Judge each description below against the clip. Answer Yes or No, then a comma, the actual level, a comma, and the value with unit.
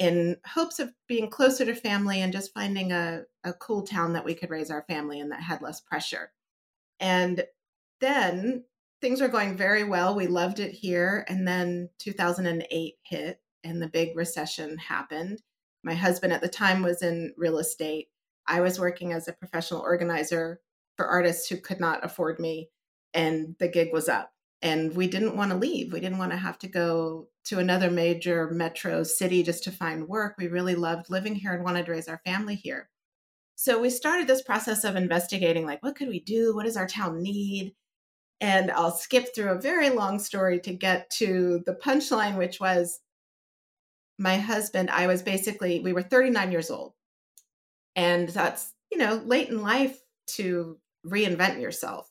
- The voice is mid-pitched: Yes, medium, 180 Hz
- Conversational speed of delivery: Yes, average, 185 wpm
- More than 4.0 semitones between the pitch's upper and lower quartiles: No, average, 3.6 semitones